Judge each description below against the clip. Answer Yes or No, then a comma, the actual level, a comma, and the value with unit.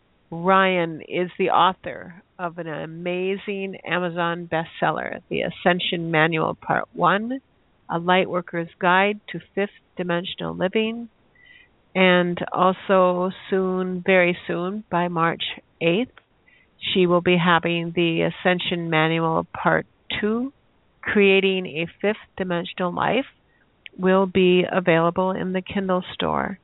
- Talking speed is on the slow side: Yes, slow, 110 wpm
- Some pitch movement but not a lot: No, narrow, 1.9 semitones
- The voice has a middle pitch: Yes, medium, 180 Hz